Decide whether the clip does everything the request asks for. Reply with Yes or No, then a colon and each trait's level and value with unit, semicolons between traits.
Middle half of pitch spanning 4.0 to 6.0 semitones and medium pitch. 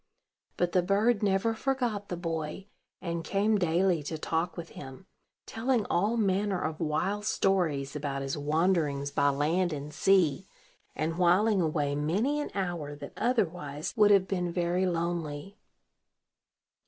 Yes: average, 4.4 semitones; medium, 175 Hz